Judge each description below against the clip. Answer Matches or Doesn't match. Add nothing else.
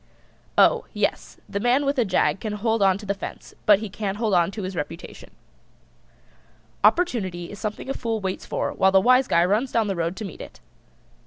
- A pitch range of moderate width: Matches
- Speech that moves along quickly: Matches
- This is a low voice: Doesn't match